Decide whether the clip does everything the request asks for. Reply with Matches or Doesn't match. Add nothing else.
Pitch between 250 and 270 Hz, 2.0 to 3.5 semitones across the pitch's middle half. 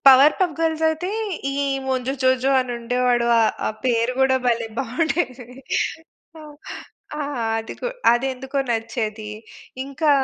Matches